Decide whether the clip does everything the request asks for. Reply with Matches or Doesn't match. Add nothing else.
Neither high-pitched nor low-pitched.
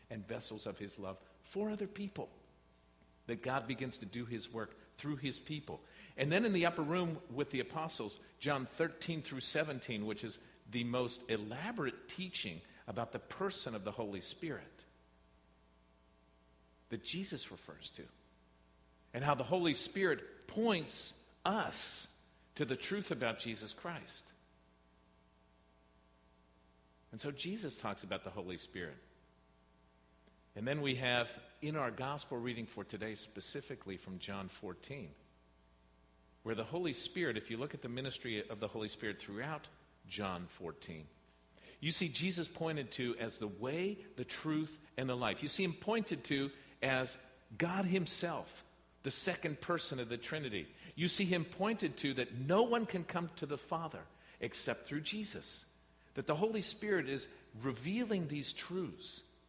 Doesn't match